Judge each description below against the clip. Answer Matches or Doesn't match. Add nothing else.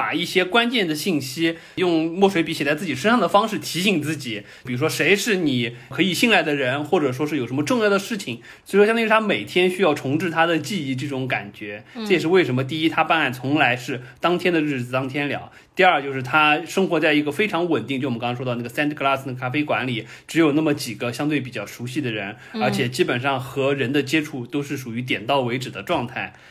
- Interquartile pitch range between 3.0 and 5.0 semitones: Matches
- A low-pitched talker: Doesn't match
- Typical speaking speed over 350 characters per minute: Matches